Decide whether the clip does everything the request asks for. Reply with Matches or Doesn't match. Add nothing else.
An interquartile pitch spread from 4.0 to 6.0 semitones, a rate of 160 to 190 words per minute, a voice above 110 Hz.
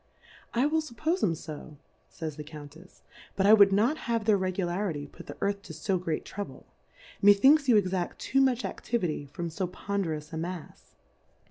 Matches